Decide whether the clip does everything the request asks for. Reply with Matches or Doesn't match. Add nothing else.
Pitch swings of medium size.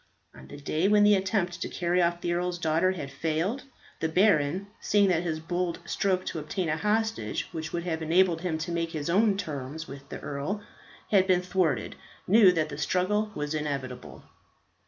Matches